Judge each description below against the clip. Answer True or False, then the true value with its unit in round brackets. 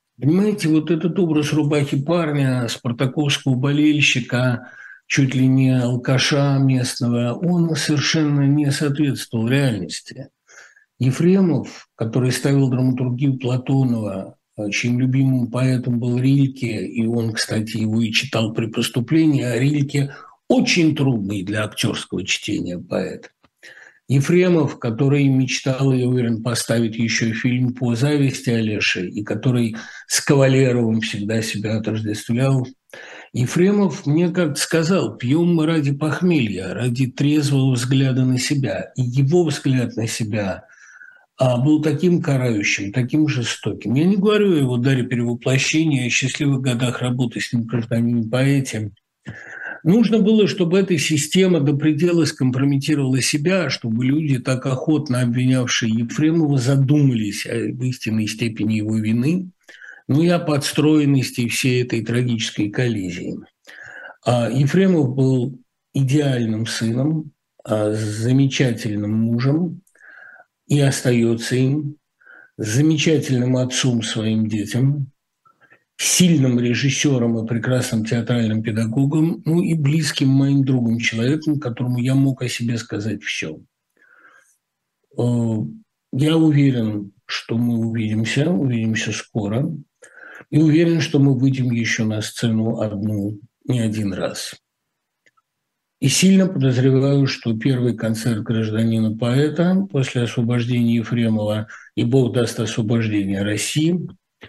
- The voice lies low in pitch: True (130 Hz)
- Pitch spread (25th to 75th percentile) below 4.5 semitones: True (4.1 semitones)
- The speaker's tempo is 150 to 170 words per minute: False (115 wpm)